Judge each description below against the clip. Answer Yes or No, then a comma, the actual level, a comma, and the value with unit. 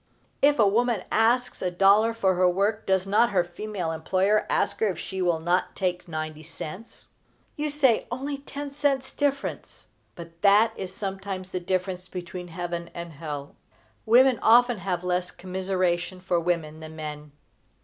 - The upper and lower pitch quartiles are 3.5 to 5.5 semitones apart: Yes, average, 4.2 semitones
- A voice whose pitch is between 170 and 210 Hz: Yes, medium, 185 Hz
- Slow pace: No, average, 160 wpm